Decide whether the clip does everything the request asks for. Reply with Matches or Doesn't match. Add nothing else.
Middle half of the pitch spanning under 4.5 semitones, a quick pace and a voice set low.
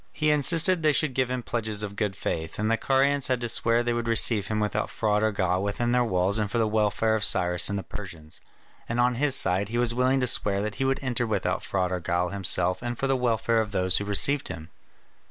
Matches